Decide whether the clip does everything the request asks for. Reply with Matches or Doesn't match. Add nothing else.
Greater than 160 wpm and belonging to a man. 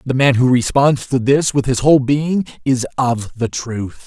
Matches